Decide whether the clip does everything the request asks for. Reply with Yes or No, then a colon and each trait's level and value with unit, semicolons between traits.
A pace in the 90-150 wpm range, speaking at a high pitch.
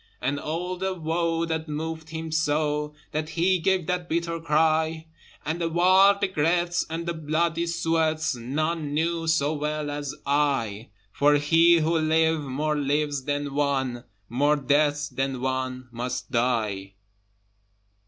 No: average, 140 wpm; medium, 155 Hz